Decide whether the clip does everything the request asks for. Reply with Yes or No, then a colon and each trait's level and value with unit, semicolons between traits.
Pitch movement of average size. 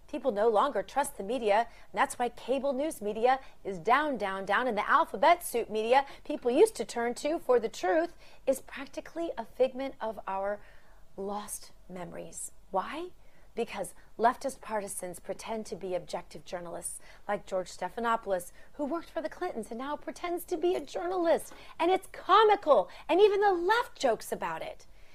No: wide, 7.1 semitones